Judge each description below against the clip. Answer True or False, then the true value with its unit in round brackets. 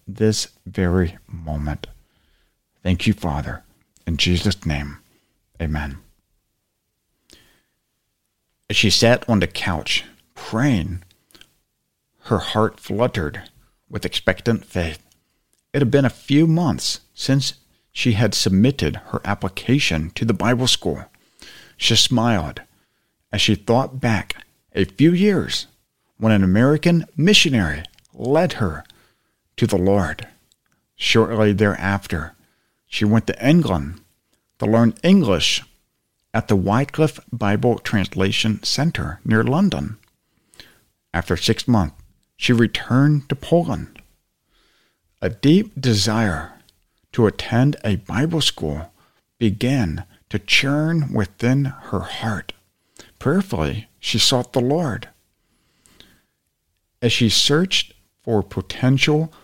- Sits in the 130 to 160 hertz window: False (110 Hz)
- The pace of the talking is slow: True (105 wpm)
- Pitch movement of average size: False (6.1 semitones)